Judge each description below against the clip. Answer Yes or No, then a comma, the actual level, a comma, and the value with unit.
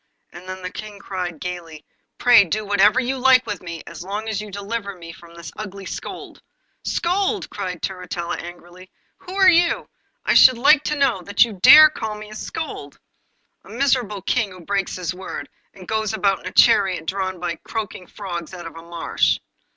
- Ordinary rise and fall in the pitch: Yes, average, 4.1 semitones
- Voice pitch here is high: Yes, high, 200 Hz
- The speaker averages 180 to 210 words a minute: Yes, average, 195 wpm